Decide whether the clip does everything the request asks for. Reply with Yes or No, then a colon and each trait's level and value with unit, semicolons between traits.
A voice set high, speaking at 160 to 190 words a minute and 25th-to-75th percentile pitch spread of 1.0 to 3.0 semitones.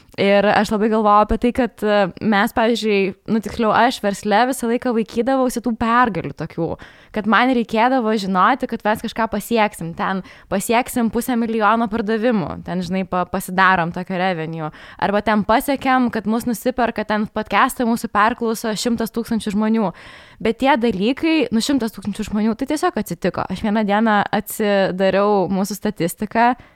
No: high, 220 Hz; average, 150 wpm; average, 2.7 semitones